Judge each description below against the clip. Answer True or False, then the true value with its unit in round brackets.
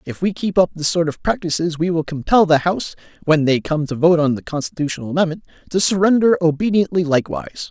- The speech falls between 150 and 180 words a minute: False (205 wpm)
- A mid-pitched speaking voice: True (170 Hz)